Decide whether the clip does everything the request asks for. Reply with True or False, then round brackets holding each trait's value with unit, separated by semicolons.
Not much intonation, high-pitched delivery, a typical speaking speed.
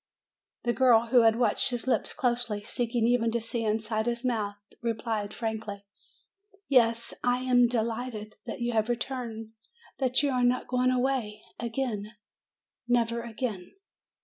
True (2.0 semitones; 235 Hz; 175 wpm)